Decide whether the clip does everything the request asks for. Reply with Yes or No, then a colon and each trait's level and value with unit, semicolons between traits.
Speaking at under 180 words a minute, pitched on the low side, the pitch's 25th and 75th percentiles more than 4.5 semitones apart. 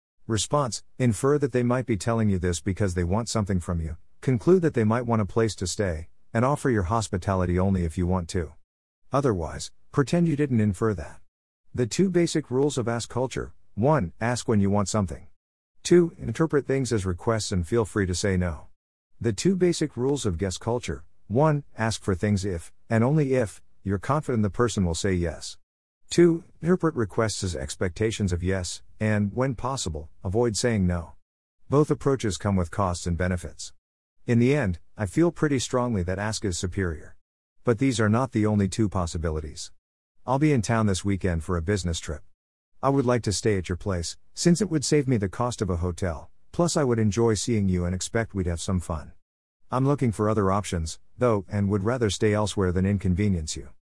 No: average, 200 wpm; low, 105 Hz; wide, 5.4 semitones